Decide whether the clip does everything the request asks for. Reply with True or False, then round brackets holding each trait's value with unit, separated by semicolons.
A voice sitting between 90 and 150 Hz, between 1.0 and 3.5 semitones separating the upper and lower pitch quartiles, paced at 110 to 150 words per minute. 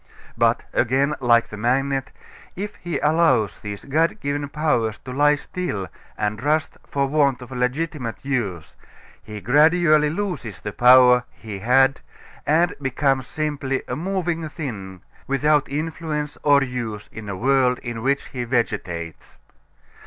False (135 Hz; 4.3 semitones; 140 wpm)